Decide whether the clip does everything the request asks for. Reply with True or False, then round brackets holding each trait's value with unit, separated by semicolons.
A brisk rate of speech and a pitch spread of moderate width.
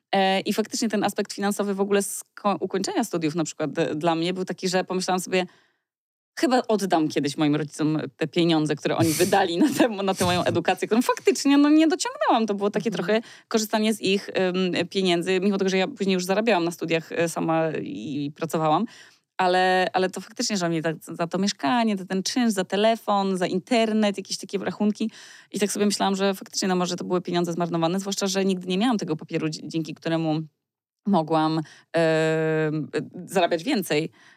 True (180 wpm; 3.8 semitones)